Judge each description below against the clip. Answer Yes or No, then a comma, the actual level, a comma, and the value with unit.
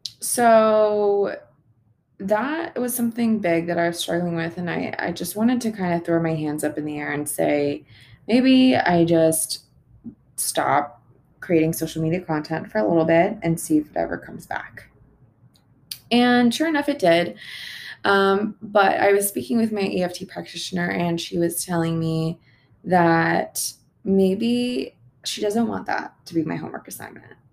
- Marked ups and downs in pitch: Yes, wide, 5.7 semitones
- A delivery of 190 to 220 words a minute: No, average, 165 wpm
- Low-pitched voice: No, medium, 170 Hz